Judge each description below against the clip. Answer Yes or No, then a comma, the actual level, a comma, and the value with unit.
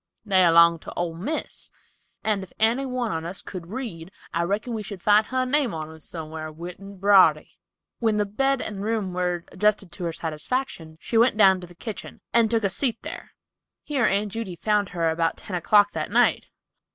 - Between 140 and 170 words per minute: No, average, 200 wpm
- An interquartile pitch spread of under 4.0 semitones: No, average, 4.6 semitones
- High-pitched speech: Yes, high, 195 Hz